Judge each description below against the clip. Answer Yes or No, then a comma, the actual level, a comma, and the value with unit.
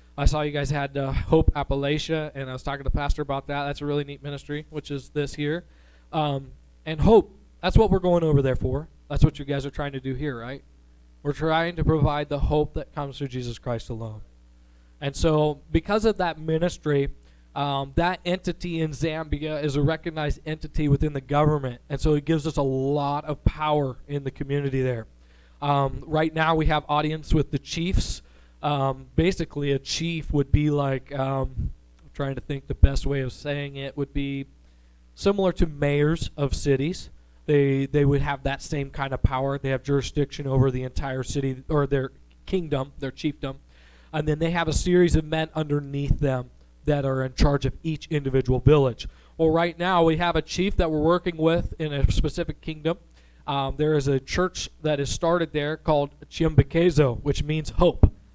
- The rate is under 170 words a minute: No, average, 195 wpm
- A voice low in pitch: No, medium, 145 Hz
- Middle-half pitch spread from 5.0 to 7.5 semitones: No, narrow, 2.6 semitones